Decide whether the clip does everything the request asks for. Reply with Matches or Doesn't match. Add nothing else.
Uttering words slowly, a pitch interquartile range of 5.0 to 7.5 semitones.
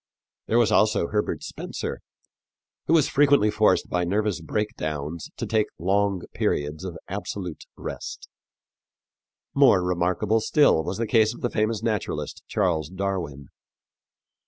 Doesn't match